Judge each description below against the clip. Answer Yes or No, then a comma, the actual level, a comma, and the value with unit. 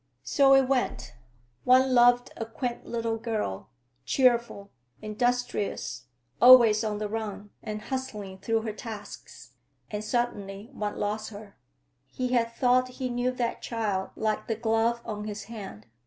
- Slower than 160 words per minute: Yes, average, 140 wpm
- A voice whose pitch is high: Yes, high, 225 Hz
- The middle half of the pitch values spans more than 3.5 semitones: No, average, 2.7 semitones